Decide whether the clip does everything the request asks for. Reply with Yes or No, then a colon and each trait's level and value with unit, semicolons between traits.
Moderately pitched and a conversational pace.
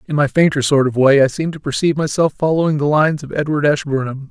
No: medium, 145 Hz; fast, 235 wpm